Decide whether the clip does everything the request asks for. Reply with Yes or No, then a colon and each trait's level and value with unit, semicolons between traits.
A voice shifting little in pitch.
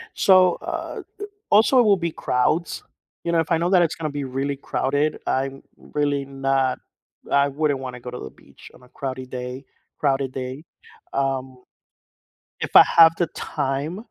No: average, 3.7 semitones